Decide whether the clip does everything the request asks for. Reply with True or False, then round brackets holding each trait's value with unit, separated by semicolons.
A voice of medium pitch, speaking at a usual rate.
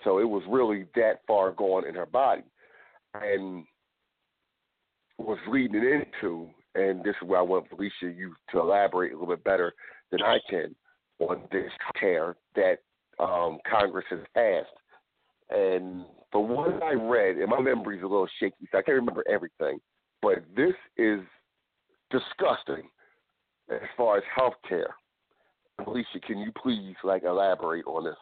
False (105 Hz; 155 wpm)